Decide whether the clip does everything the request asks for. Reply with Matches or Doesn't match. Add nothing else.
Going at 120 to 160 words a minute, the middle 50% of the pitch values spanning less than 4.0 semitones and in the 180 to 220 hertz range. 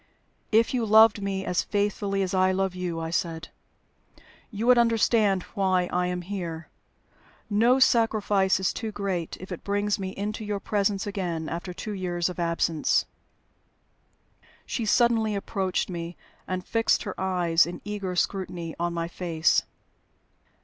Matches